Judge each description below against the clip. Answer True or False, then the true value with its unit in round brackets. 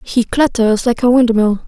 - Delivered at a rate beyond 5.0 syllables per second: False (4.5 syllables/s)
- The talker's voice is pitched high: True (235 Hz)